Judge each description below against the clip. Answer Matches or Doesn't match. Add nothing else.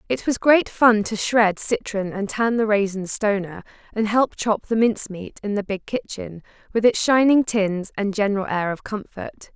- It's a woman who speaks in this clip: Matches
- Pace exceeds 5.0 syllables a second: Doesn't match